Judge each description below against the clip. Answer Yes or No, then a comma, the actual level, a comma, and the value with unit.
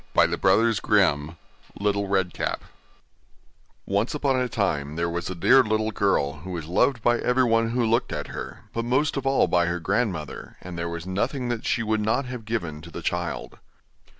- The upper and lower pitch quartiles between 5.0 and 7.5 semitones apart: Yes, wide, 5.5 semitones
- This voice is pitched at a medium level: No, low, 105 Hz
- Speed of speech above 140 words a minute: Yes, average, 195 wpm